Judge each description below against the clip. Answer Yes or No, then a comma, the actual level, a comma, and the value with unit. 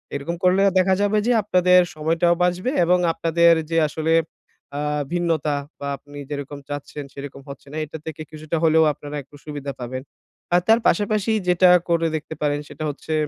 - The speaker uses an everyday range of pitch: Yes, average, 3.6 semitones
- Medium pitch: Yes, medium, 160 Hz